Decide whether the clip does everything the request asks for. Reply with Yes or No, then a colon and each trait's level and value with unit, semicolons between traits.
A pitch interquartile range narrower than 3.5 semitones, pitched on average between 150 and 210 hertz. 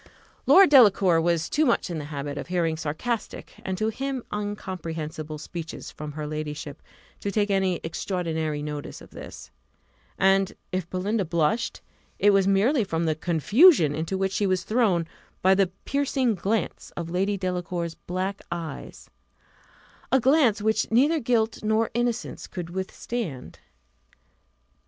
No: average, 5.0 semitones; high, 190 Hz